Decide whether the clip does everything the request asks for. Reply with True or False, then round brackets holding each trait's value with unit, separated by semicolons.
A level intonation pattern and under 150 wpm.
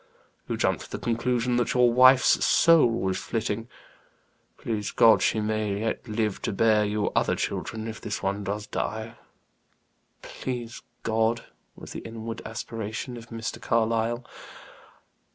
True (1.6 semitones; 140 wpm)